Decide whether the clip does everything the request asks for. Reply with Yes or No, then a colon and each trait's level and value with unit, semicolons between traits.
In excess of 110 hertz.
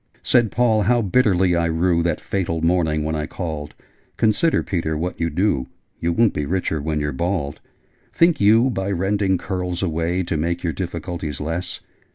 No: very low, 85 Hz